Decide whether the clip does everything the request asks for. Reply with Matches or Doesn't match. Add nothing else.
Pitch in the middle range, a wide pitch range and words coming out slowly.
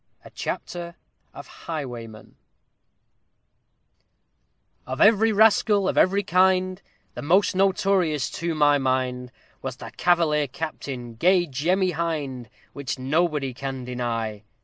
Matches